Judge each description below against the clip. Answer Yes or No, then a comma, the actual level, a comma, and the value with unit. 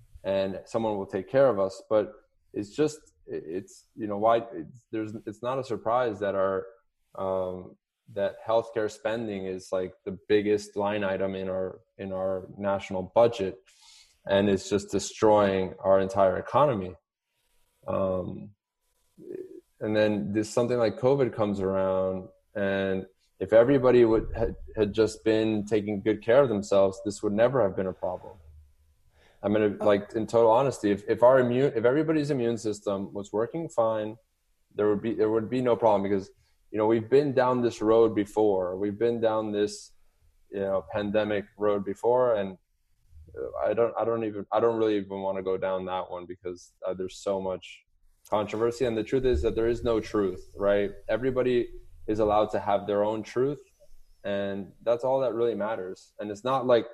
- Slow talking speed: No, average, 175 wpm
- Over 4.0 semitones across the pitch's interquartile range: No, average, 3.2 semitones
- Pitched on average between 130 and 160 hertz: No, low, 105 Hz